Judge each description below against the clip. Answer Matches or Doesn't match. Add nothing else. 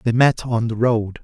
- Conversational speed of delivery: Doesn't match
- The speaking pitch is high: Doesn't match